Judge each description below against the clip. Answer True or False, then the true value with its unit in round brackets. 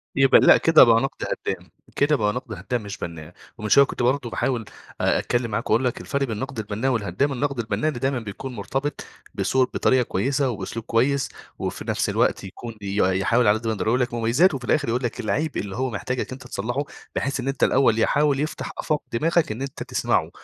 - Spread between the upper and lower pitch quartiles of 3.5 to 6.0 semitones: True (3.8 semitones)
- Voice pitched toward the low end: True (125 Hz)